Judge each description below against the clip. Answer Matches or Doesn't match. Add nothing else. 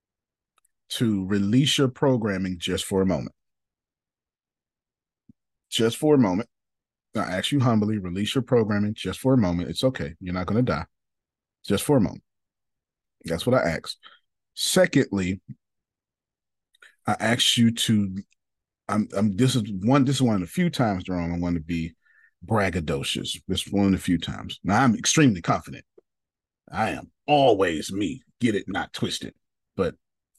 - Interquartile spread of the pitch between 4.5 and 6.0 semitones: Matches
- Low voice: Matches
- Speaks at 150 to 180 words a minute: Matches